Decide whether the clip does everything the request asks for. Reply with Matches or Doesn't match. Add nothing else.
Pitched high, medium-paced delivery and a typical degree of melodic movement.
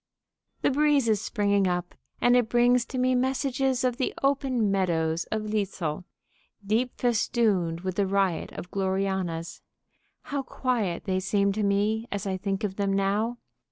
Matches